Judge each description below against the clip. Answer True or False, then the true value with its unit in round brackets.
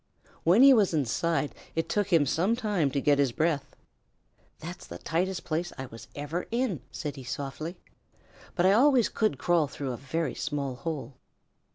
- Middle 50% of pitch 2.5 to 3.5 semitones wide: False (4.9 semitones)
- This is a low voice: False (165 Hz)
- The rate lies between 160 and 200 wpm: True (175 wpm)